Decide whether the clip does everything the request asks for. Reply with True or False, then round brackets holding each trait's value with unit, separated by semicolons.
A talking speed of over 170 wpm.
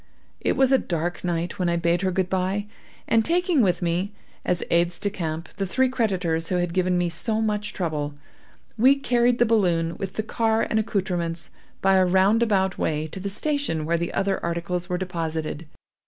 True (190 wpm)